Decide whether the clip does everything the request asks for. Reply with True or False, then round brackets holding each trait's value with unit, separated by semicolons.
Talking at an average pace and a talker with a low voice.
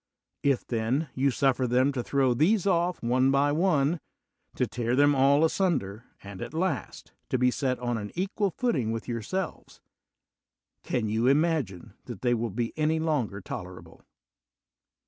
True (160 wpm; 130 Hz)